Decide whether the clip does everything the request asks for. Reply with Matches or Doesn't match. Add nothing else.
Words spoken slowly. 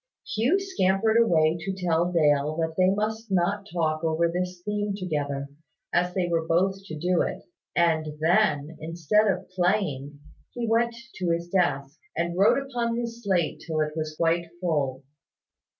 Doesn't match